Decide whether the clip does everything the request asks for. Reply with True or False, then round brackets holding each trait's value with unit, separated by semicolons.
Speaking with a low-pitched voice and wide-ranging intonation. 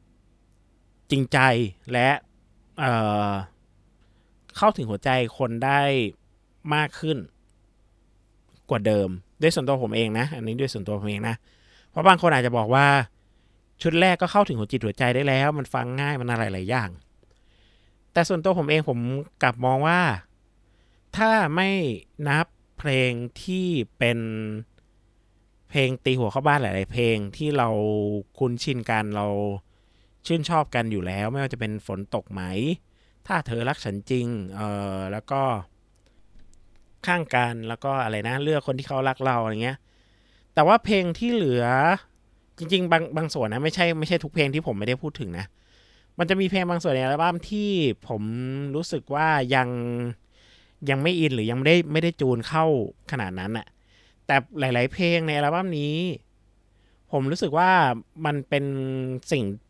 True (125 Hz; 6.2 semitones)